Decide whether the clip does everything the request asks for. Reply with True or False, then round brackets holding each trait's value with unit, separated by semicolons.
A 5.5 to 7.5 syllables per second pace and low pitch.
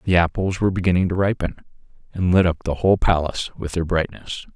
True (6.5 syllables/s; 90 Hz)